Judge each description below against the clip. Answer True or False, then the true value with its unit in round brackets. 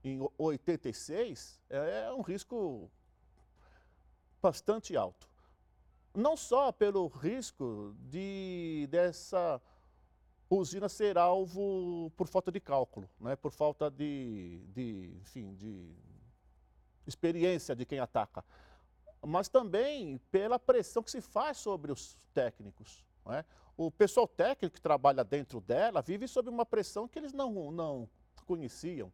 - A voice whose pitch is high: False (165 Hz)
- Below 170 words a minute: True (120 wpm)